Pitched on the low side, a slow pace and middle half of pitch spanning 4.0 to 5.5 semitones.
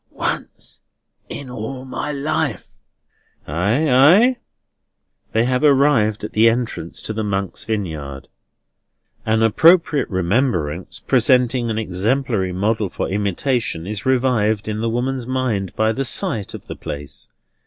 Yes: low, 115 Hz; slow, 130 wpm; average, 4.6 semitones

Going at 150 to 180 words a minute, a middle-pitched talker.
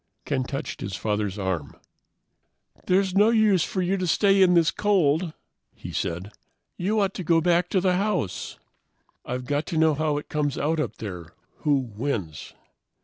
Yes: average, 170 wpm; medium, 155 Hz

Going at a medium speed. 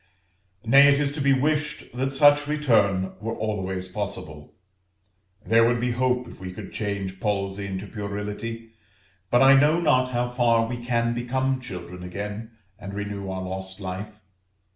Yes: average, 160 wpm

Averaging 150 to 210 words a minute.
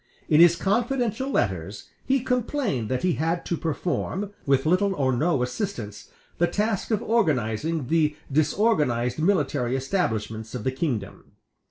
No: average, 140 wpm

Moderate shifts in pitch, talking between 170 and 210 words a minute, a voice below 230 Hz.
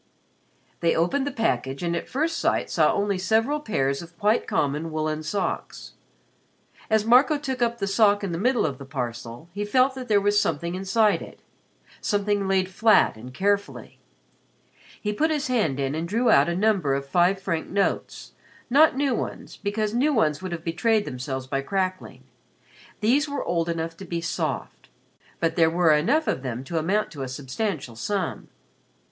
No: wide, 6.0 semitones; average, 180 wpm; high, 190 Hz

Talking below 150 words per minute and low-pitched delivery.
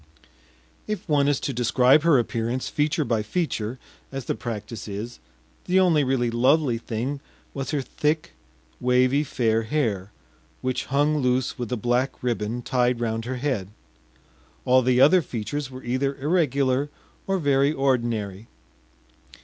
Yes: average, 140 wpm; low, 130 Hz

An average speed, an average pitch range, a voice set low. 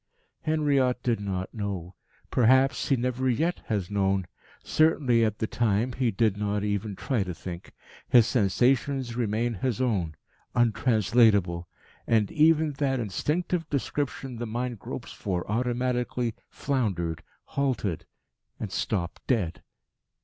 No: slow, 125 wpm; average, 4.2 semitones; low, 115 Hz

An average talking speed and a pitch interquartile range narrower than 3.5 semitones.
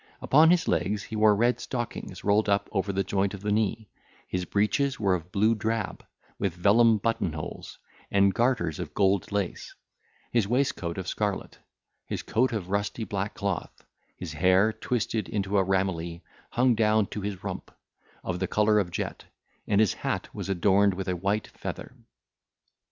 Yes: average, 170 wpm; narrow, 2.5 semitones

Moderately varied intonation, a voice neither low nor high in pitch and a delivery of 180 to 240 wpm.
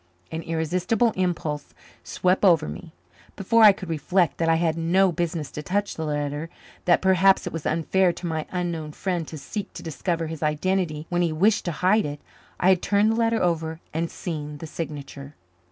Yes: average, 3.1 semitones; medium, 170 Hz; average, 190 wpm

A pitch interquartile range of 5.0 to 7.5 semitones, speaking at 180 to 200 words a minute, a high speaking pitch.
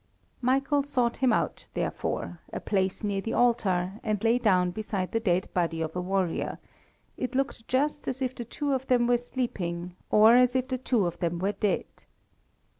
Yes: average, 5.3 semitones; average, 190 wpm; high, 225 Hz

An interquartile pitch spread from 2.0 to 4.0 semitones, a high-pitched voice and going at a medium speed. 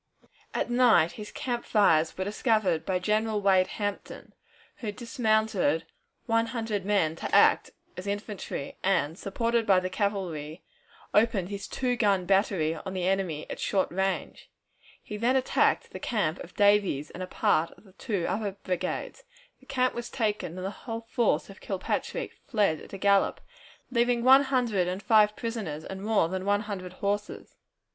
Yes: average, 3.5 semitones; high, 205 Hz; average, 165 wpm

